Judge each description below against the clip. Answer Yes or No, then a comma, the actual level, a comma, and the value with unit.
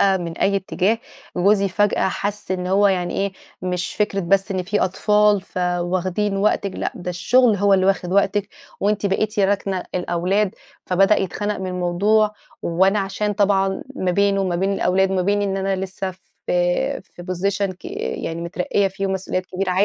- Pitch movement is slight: Yes, narrow, 1.7 semitones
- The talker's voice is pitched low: No, high, 195 Hz